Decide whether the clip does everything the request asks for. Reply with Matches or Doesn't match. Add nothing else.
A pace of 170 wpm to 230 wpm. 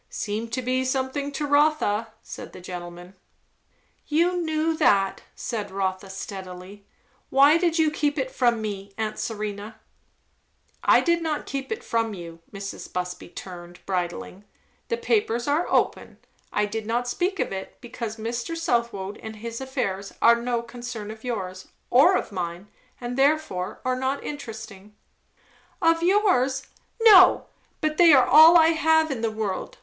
Doesn't match